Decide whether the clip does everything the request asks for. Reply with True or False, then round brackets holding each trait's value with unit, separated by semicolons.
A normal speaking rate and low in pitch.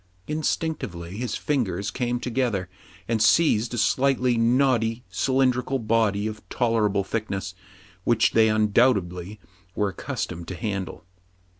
False (120 wpm; 115 Hz)